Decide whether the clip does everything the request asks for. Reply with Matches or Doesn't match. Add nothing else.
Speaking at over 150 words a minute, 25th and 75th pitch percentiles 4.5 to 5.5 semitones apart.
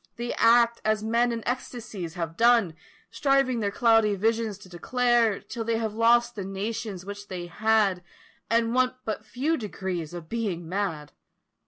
Doesn't match